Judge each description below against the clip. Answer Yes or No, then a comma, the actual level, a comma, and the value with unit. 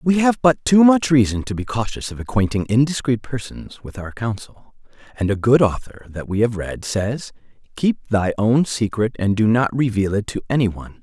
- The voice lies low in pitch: Yes, low, 120 Hz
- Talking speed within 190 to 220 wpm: Yes, average, 200 wpm